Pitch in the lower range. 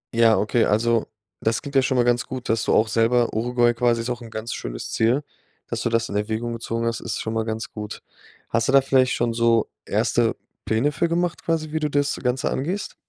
Yes: low, 120 Hz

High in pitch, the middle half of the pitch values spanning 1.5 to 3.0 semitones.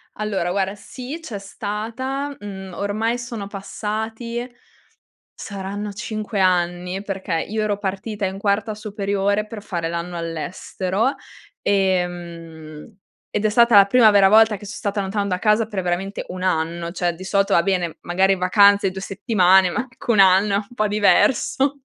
Yes: high, 200 Hz; narrow, 2.5 semitones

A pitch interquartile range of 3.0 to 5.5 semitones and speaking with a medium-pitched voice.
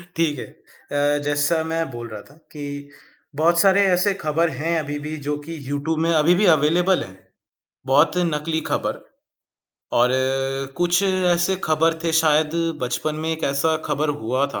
No: narrow, 2.6 semitones; medium, 160 Hz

